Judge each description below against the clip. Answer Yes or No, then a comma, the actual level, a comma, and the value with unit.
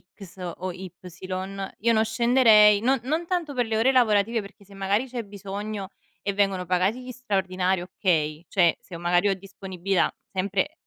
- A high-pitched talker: Yes, high, 200 Hz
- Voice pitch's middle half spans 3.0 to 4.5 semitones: Yes, average, 3.7 semitones